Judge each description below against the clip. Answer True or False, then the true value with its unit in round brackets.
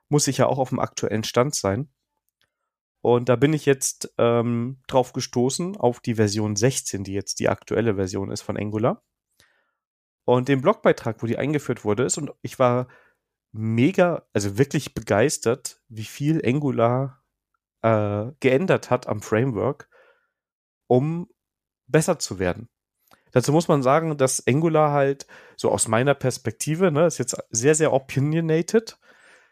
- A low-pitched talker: True (130 Hz)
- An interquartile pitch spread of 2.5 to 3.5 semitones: False (4.7 semitones)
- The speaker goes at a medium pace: True (150 wpm)